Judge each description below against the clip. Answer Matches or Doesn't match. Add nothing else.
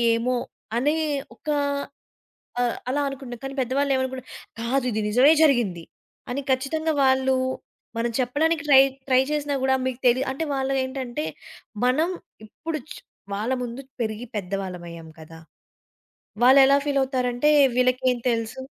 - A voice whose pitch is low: Doesn't match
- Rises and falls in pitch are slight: Matches